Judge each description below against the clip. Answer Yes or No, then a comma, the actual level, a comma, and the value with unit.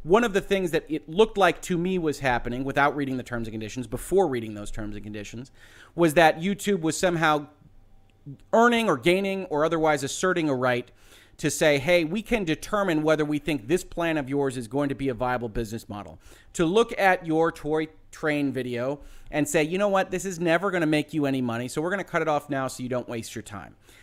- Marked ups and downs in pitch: Yes, wide, 5.8 semitones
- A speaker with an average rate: No, fast, 230 wpm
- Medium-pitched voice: Yes, medium, 150 Hz